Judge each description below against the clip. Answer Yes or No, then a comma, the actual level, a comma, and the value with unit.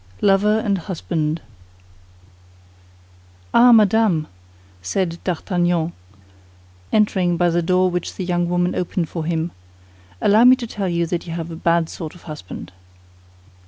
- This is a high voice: No, medium, 175 Hz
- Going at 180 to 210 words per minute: No, average, 140 wpm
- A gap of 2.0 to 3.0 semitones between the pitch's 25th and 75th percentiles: Yes, average, 2.7 semitones